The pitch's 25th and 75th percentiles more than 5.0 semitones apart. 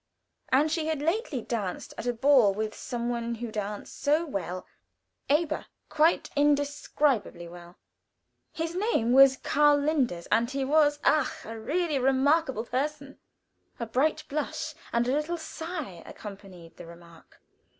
Yes: wide, 5.4 semitones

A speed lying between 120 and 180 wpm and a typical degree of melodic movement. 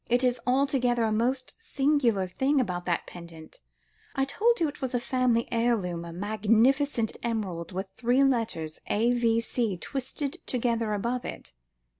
Yes: average, 145 wpm; average, 4.2 semitones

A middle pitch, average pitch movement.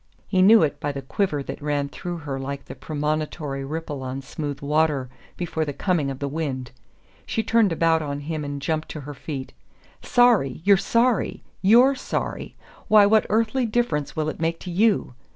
No: medium, 155 Hz; wide, 5.8 semitones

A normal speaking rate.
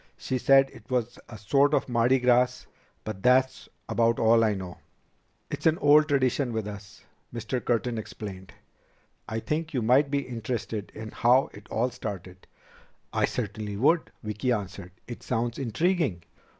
Yes: average, 155 wpm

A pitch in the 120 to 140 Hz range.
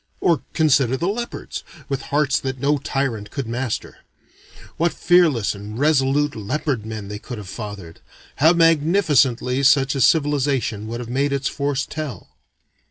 Yes: low, 135 Hz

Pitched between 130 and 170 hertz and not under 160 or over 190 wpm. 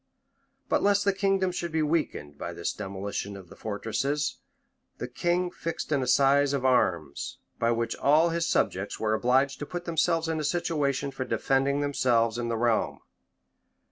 Yes: medium, 140 Hz; average, 170 wpm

